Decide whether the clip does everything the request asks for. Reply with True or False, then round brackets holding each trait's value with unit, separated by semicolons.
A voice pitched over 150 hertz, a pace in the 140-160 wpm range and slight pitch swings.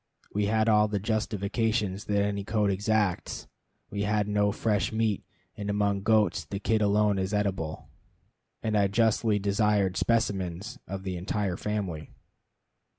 False (105 Hz; 145 wpm; 1.4 semitones)